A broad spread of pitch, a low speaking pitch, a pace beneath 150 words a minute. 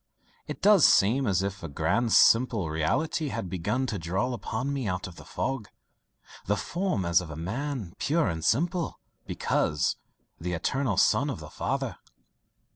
No: wide, 7.2 semitones; low, 105 Hz; average, 165 wpm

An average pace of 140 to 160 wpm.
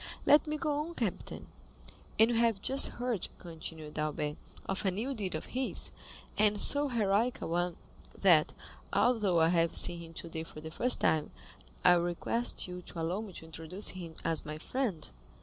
No: average, 180 wpm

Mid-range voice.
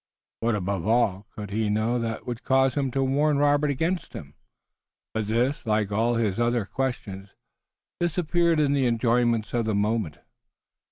No: low, 120 Hz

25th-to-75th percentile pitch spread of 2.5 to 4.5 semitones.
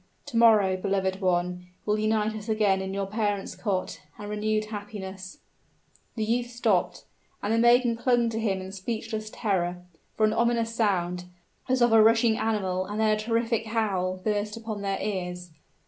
Yes: average, 2.9 semitones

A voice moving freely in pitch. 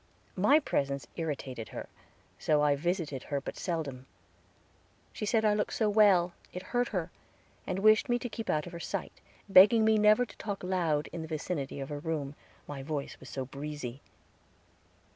Yes: wide, 6.5 semitones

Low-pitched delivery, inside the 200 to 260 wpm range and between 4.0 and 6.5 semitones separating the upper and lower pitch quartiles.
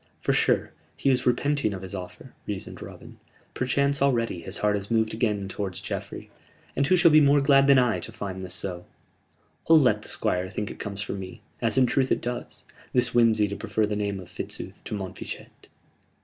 Yes: low, 110 Hz; fast, 205 wpm; average, 4.9 semitones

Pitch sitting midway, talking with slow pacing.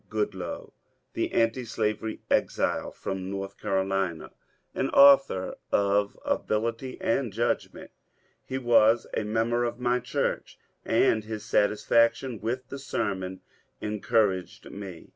No: low, 110 Hz; slow, 120 wpm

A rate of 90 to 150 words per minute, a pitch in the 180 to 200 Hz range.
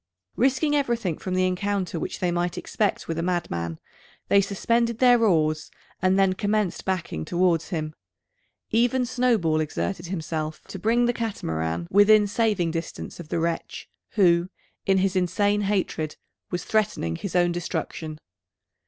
Yes: average, 145 wpm; medium, 185 Hz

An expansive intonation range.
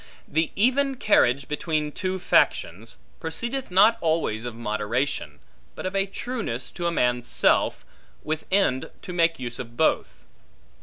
Yes: wide, 8.0 semitones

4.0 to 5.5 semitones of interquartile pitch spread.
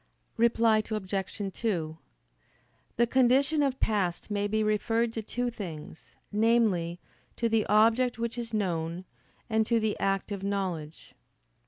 No: average, 3.2 semitones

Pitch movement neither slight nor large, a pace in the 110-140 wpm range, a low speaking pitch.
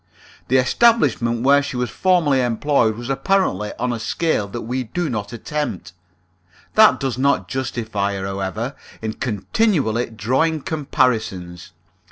Yes: average, 4.8 semitones; slow, 135 wpm; low, 125 Hz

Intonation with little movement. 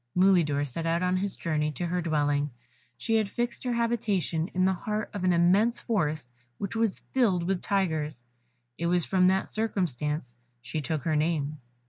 No: average, 4.5 semitones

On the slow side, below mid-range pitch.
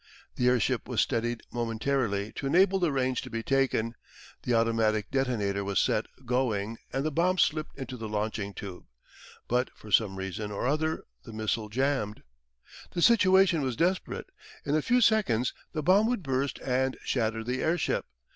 No: average, 165 wpm; low, 125 Hz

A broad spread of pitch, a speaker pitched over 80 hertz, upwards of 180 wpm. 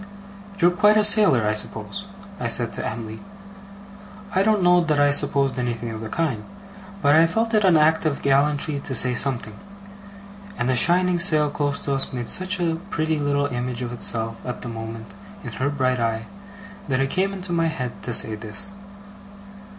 Yes: wide, 6.0 semitones; medium, 140 Hz; average, 190 wpm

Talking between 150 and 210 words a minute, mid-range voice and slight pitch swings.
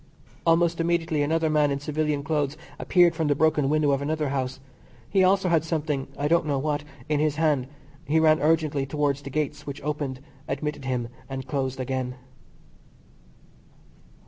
Yes: average, 165 wpm; medium, 150 Hz; narrow, 2.3 semitones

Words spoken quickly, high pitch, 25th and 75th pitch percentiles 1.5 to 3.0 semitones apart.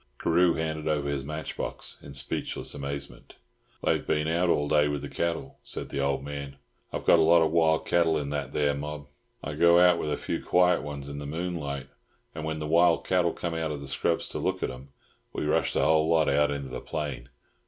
No: fast, 225 wpm; very low, 75 Hz; narrow, 2.4 semitones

